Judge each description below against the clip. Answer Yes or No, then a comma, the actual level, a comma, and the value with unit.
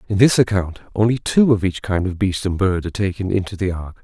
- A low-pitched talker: Yes, low, 100 Hz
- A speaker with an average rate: No, fast, 255 wpm